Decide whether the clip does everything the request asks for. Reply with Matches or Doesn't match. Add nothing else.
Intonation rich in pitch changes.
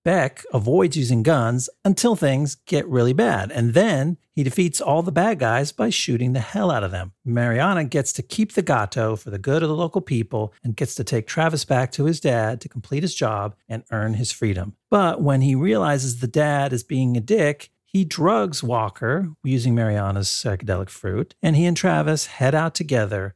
Matches